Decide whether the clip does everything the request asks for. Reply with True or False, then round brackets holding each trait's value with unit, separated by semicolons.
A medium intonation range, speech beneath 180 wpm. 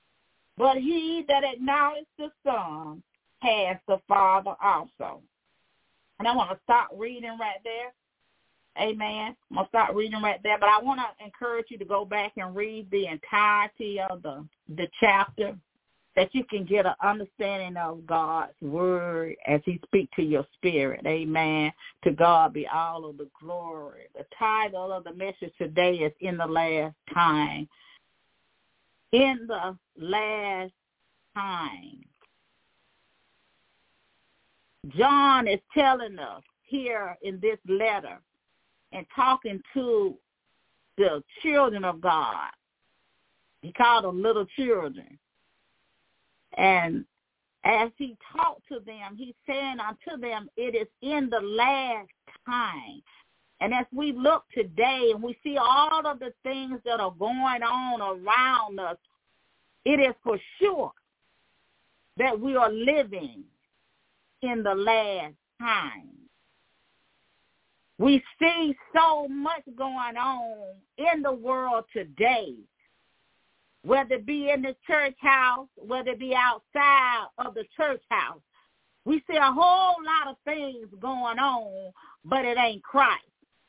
False (5.9 semitones; 135 wpm)